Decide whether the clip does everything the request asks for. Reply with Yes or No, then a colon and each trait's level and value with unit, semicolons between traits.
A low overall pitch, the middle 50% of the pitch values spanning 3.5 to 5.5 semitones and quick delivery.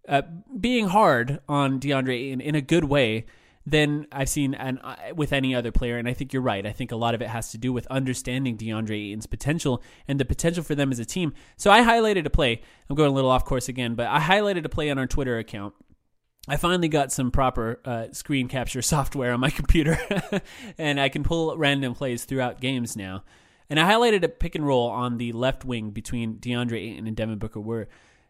Yes: low, 130 Hz; average, 3.8 semitones; fast, 225 wpm